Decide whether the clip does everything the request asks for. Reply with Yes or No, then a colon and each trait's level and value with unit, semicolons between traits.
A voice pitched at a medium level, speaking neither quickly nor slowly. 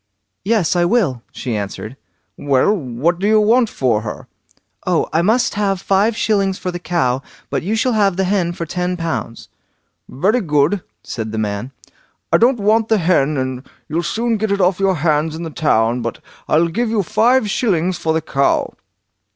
Yes: medium, 175 Hz; average, 190 wpm